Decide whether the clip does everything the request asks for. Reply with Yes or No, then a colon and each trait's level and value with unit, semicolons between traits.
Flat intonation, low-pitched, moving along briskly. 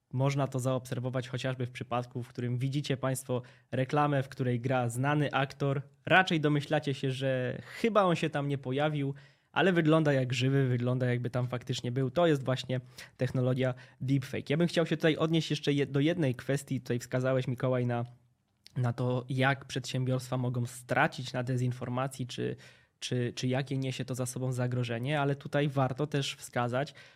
Yes: narrow, 2.0 semitones; low, 130 Hz; fast, 170 wpm